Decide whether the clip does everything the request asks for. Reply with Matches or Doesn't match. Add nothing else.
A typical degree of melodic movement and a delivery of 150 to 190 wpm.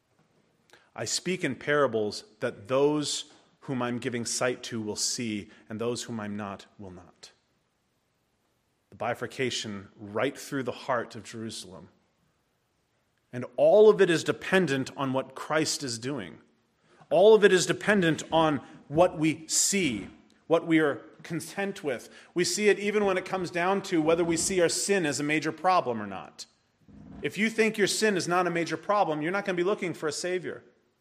Doesn't match